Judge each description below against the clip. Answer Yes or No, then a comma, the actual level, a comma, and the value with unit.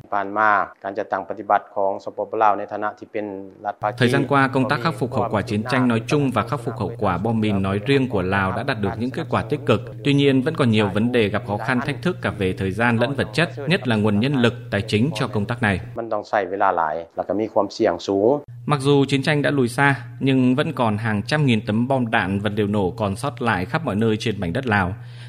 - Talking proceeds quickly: No, average, 215 wpm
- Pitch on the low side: Yes, low, 115 Hz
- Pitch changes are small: No, average, 4.6 semitones